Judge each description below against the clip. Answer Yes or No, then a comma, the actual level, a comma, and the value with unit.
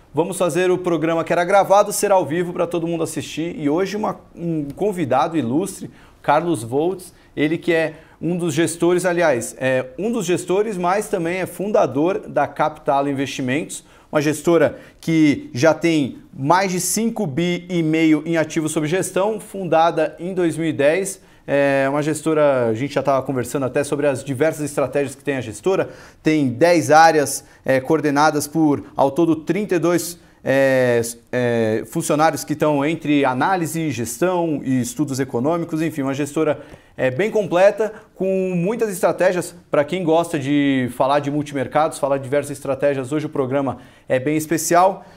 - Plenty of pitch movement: No, average, 3.5 semitones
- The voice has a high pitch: No, medium, 160 Hz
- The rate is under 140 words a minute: No, average, 160 wpm